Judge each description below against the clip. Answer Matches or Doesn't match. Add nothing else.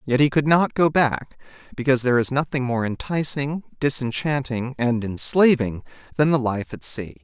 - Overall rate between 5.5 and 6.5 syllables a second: Doesn't match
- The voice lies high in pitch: Doesn't match